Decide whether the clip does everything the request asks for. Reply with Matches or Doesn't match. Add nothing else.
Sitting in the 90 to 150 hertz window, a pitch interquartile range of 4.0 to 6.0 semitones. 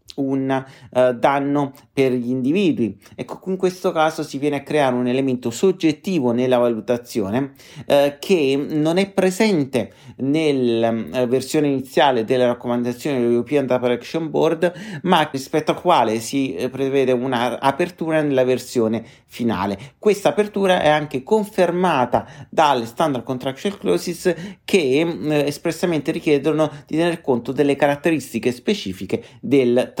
Matches